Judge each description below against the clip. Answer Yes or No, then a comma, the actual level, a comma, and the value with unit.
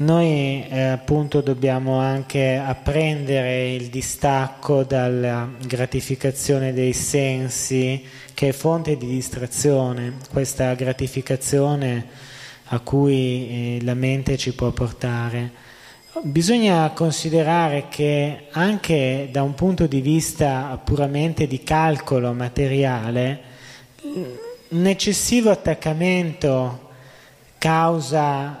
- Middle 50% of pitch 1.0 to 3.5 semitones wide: Yes, average, 2.9 semitones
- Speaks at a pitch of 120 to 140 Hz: Yes, low, 135 Hz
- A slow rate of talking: Yes, slow, 90 wpm